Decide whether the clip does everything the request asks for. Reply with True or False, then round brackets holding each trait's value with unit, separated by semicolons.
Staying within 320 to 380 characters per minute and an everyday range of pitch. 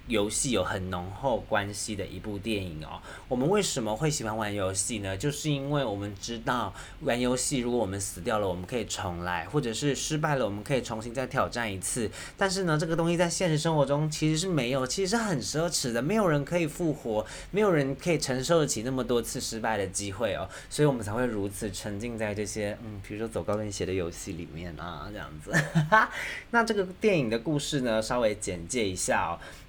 False (330 characters per minute; 6.6 semitones)